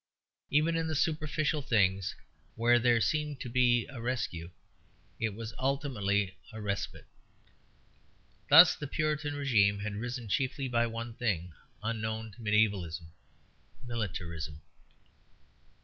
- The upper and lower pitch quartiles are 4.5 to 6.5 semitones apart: Yes, average, 5.3 semitones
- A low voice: Yes, low, 115 Hz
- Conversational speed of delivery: No, slow, 115 wpm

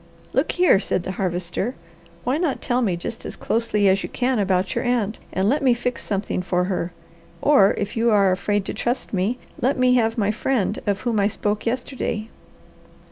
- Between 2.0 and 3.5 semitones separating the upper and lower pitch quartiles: No, average, 4.2 semitones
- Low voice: No, high, 215 Hz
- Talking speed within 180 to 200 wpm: Yes, average, 195 wpm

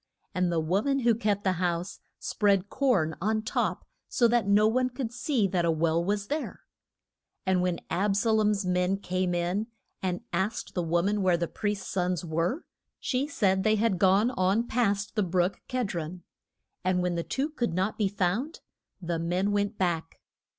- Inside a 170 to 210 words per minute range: Yes, average, 185 wpm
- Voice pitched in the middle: No, high, 195 Hz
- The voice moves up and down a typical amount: Yes, average, 3.5 semitones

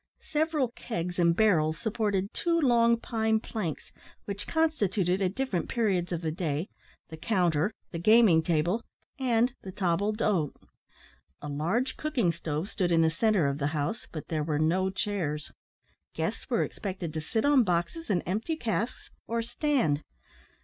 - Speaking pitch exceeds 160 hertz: Yes, high, 190 Hz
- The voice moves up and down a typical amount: No, wide, 5.8 semitones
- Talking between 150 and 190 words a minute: Yes, average, 155 wpm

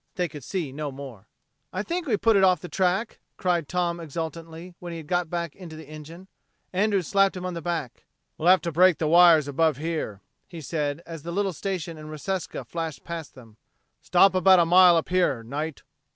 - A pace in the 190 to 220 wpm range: Yes, fast, 205 wpm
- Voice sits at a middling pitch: Yes, medium, 170 Hz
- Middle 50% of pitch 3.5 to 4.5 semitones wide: No, average, 3.0 semitones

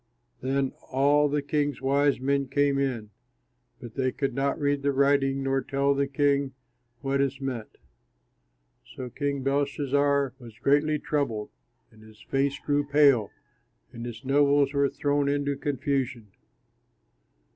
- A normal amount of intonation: No, narrow, 1.3 semitones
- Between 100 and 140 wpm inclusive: Yes, slow, 135 wpm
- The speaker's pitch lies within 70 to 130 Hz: No, medium, 140 Hz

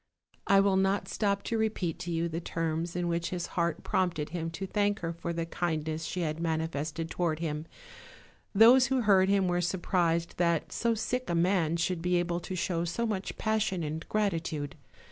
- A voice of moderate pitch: Yes, medium, 175 Hz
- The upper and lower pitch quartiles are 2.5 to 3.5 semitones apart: Yes, average, 2.9 semitones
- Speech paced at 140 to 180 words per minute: No, average, 195 wpm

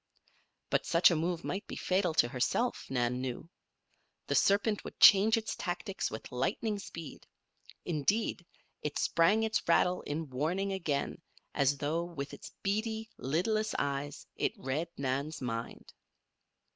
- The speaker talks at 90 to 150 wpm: Yes, average, 140 wpm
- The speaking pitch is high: No, medium, 165 Hz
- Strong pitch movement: Yes, wide, 6.1 semitones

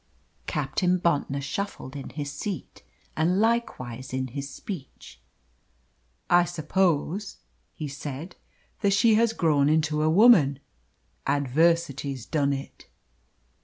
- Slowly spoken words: Yes, slow, 110 wpm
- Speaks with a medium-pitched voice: Yes, medium, 155 Hz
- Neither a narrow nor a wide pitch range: Yes, average, 4.7 semitones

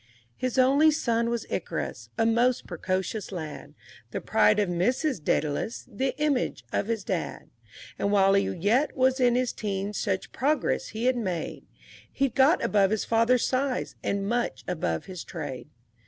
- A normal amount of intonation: Yes, average, 4.8 semitones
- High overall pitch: Yes, high, 225 Hz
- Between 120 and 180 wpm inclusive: Yes, average, 165 wpm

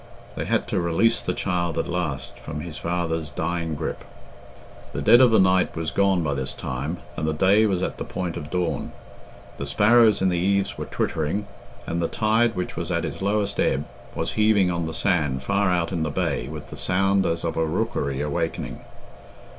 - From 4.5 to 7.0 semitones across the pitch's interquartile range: No, average, 3.8 semitones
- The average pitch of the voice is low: Yes, very low, 85 Hz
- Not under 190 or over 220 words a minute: Yes, average, 200 wpm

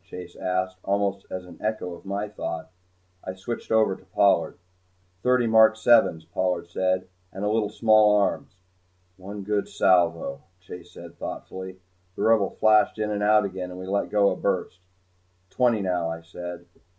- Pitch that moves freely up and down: No, average, 2.8 semitones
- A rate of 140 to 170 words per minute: Yes, average, 165 wpm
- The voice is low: Yes, very low, 95 Hz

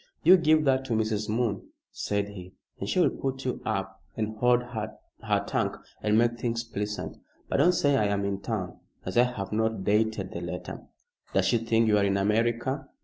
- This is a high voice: No, low, 110 Hz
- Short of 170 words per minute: No, average, 200 wpm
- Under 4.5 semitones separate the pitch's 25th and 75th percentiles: Yes, average, 3.1 semitones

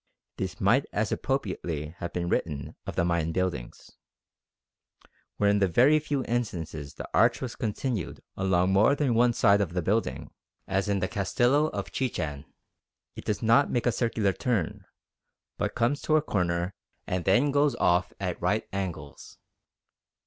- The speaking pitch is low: Yes, low, 100 Hz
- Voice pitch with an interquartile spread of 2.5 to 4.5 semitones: No, wide, 5.5 semitones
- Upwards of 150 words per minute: Yes, average, 160 wpm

